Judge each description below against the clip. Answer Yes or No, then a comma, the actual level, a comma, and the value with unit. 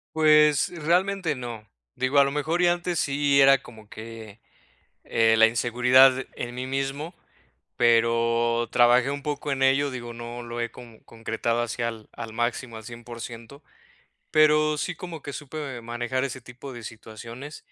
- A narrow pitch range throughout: No, average, 3.5 semitones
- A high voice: No, low, 125 Hz